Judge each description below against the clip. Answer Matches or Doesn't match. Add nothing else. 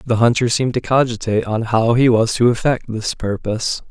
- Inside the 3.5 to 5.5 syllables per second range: Doesn't match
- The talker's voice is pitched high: Doesn't match